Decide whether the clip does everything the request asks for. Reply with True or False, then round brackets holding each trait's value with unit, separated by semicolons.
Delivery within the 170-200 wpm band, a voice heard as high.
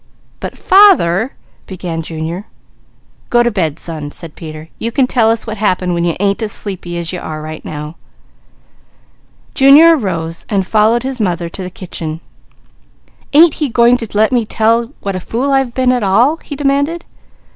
True (180 wpm; 210 Hz)